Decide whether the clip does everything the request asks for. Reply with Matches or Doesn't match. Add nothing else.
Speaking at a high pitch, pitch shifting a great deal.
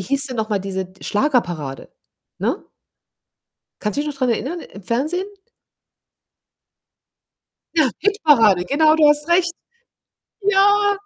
Matches